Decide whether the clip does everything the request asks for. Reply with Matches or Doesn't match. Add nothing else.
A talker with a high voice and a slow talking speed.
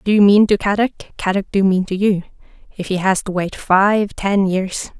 Doesn't match